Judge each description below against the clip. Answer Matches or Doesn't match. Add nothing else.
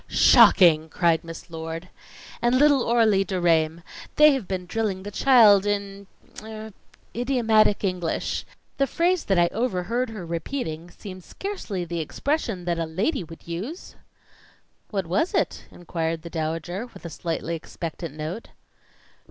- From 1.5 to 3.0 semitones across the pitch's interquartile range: Doesn't match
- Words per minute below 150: Matches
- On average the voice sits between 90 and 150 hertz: Doesn't match